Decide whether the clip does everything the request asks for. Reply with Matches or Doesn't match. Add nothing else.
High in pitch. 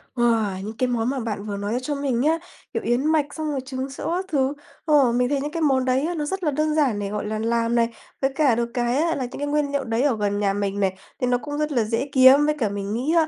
Matches